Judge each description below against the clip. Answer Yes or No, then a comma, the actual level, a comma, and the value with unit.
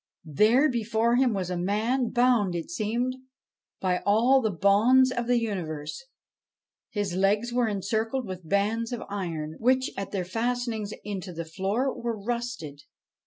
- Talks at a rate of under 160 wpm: Yes, average, 150 wpm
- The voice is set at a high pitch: Yes, high, 215 Hz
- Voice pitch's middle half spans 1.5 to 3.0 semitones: No, average, 4.3 semitones